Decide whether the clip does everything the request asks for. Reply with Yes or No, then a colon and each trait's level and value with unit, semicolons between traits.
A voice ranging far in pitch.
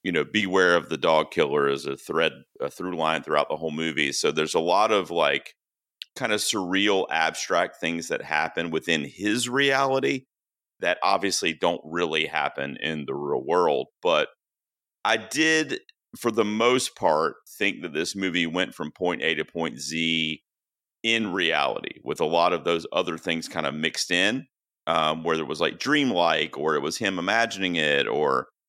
Yes: wide, 7.9 semitones